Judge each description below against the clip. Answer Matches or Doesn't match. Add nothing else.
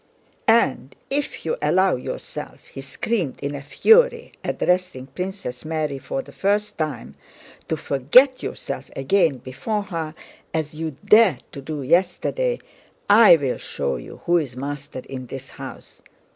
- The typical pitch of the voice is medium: Matches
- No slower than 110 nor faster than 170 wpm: Matches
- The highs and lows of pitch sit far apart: Matches